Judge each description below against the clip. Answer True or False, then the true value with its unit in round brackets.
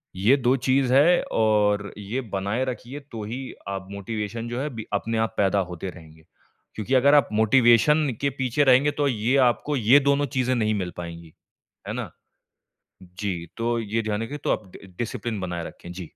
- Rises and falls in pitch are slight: False (4.6 semitones)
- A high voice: False (115 Hz)